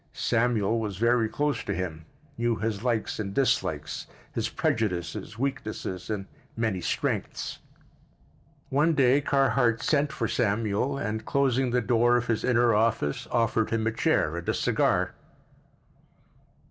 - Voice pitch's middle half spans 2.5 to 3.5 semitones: Yes, average, 3.0 semitones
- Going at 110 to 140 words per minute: Yes, slow, 135 wpm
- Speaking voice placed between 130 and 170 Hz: No, low, 115 Hz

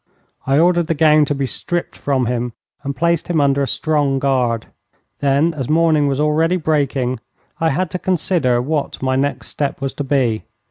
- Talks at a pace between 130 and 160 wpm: No, average, 185 wpm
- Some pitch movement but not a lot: Yes, average, 3.1 semitones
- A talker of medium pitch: Yes, medium, 145 Hz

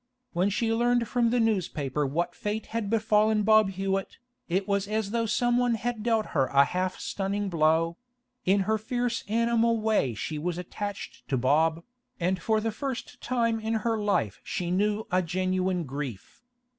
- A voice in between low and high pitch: No, high, 205 Hz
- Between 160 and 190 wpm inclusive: Yes, average, 170 wpm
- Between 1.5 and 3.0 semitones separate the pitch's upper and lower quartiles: No, average, 4.3 semitones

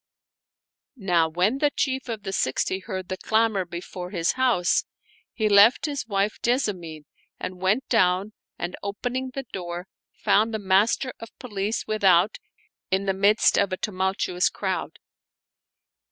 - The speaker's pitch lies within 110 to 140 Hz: No, high, 200 Hz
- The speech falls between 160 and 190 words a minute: No, average, 140 wpm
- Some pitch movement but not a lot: Yes, average, 3.6 semitones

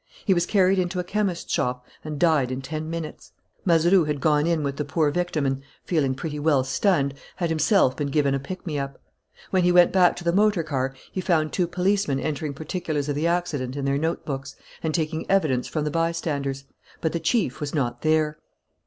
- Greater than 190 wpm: Yes, fast, 205 wpm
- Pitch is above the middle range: No, medium, 155 Hz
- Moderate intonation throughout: Yes, average, 3.9 semitones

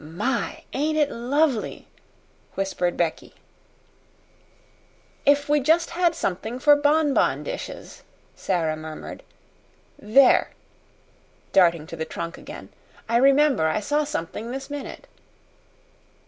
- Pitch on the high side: Yes, very high, 260 Hz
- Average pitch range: No, wide, 8.8 semitones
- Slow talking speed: Yes, slow, 105 wpm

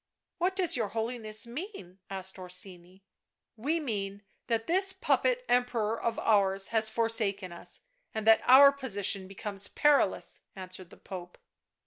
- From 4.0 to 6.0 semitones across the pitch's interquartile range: Yes, average, 4.6 semitones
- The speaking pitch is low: No, high, 220 Hz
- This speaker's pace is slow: No, average, 145 wpm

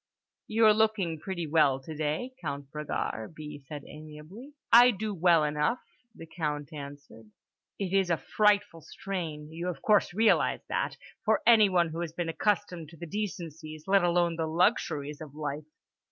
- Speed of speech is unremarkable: Yes, average, 150 wpm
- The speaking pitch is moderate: Yes, medium, 165 Hz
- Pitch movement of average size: Yes, average, 4.7 semitones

